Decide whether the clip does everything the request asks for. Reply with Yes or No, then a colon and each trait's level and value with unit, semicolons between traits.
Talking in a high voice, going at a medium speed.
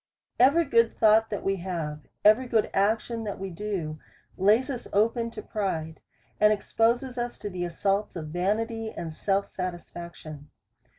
Yes: high, 205 Hz; average, 160 wpm